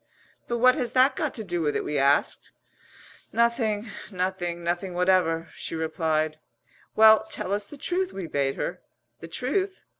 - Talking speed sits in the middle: Yes, average, 160 wpm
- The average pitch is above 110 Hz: Yes, medium, 185 Hz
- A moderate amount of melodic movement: No, wide, 6.2 semitones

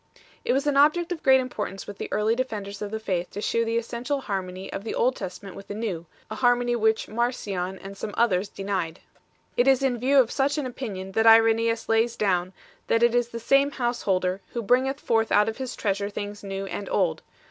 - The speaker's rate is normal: No, fast, 220 wpm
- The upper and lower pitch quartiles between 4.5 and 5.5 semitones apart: No, average, 3.7 semitones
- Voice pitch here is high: Yes, high, 225 Hz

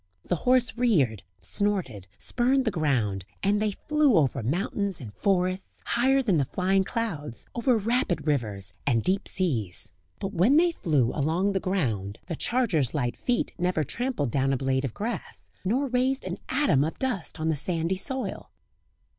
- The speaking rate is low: No, average, 165 wpm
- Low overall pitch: No, medium, 185 Hz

